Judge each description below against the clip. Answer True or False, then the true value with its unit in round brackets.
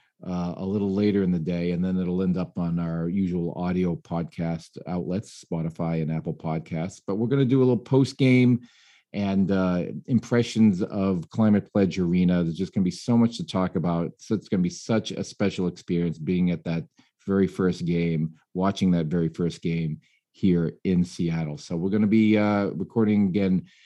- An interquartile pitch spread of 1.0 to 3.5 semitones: True (3.0 semitones)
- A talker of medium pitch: False (90 Hz)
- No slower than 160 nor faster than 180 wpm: False (195 wpm)